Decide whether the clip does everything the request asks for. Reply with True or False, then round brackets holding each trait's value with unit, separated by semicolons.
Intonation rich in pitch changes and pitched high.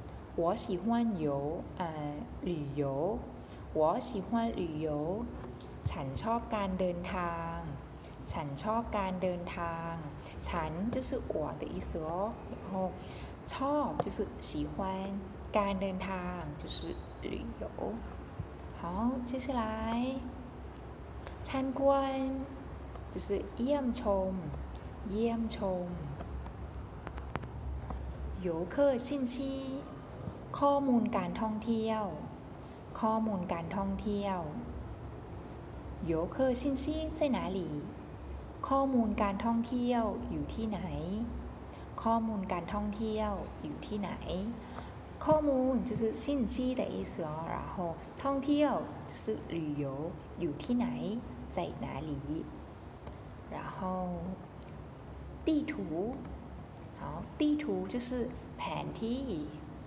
True (6.3 semitones; 210 Hz)